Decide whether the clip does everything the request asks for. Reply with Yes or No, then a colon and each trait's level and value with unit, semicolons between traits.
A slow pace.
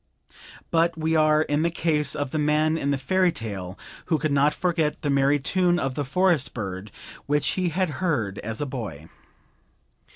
No: average, 185 wpm